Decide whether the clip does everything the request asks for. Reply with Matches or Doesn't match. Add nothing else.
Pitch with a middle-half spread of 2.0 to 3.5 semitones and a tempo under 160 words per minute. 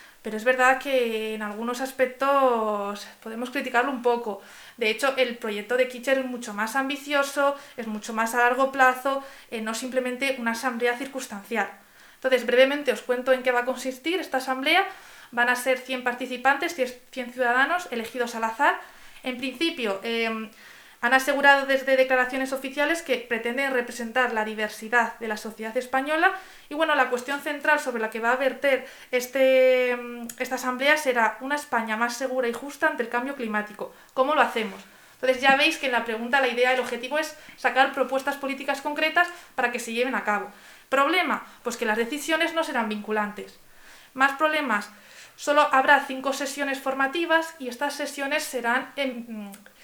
Doesn't match